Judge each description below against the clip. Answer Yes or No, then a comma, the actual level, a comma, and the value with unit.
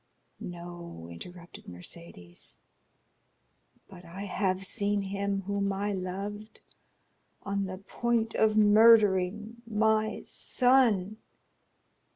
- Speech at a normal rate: No, slow, 90 wpm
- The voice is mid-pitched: No, high, 200 Hz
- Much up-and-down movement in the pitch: No, average, 2.8 semitones